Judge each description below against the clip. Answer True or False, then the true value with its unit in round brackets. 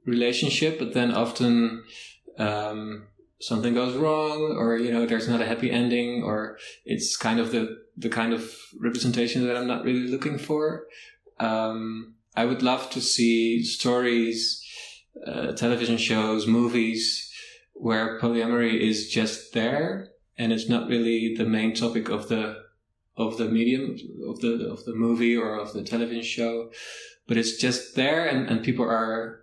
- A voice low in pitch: True (115 Hz)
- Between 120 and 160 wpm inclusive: True (155 wpm)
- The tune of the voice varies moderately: False (1.4 semitones)